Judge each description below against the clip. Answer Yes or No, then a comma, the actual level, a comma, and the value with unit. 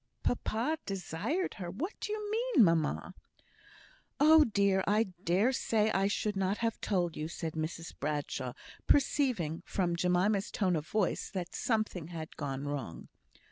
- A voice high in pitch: Yes, high, 195 Hz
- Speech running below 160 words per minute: Yes, average, 145 wpm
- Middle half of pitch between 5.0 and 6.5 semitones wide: Yes, average, 5.3 semitones